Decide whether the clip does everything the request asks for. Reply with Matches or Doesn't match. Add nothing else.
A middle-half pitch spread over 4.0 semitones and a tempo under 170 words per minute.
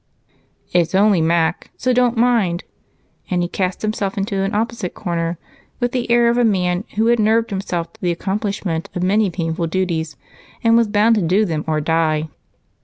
Doesn't match